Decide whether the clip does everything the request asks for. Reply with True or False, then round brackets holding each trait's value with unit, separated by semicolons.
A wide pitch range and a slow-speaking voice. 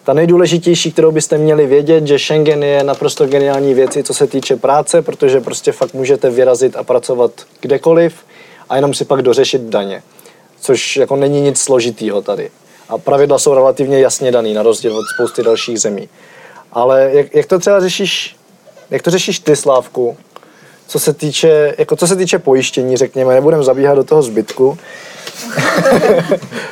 False (6.7 semitones; 165 wpm)